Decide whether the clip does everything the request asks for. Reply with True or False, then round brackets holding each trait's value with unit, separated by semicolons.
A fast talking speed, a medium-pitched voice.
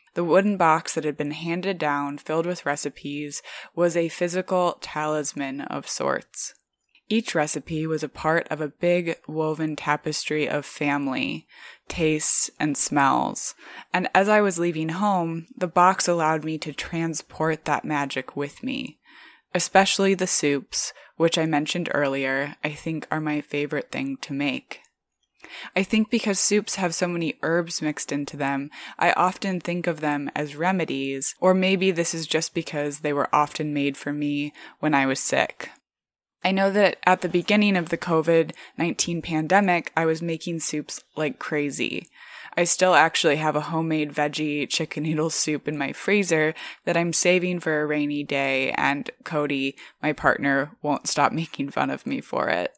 False (165 wpm; 160 Hz)